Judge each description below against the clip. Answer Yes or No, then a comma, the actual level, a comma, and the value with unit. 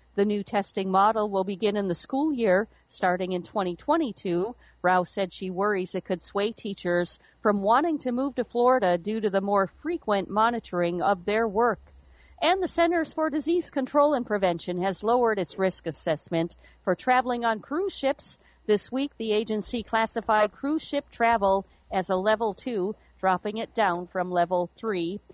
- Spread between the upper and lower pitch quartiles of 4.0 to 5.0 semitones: Yes, average, 4.6 semitones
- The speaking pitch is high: Yes, high, 210 Hz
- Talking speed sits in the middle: Yes, average, 170 wpm